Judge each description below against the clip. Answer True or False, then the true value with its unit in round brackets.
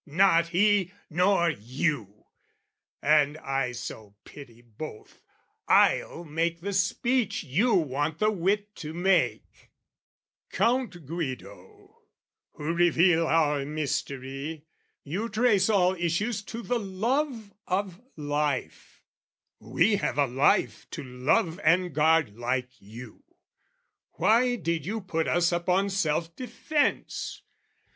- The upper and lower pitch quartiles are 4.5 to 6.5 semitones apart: True (5.6 semitones)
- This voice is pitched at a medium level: True (170 Hz)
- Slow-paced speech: True (110 wpm)